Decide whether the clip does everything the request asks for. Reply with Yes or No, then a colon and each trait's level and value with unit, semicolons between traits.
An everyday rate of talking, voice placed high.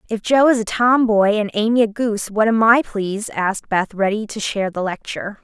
No: fast, 220 wpm; high, 215 Hz